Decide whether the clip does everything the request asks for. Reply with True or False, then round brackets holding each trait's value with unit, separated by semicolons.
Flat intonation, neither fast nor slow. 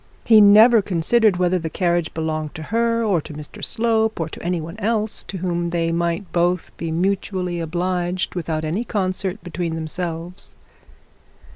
False (3.5 semitones; 160 wpm)